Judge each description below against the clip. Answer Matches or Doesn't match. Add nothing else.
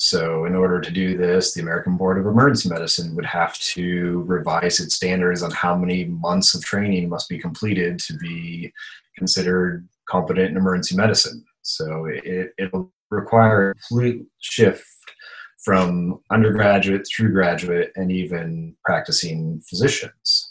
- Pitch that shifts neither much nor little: Doesn't match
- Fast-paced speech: Doesn't match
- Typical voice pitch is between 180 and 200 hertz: Doesn't match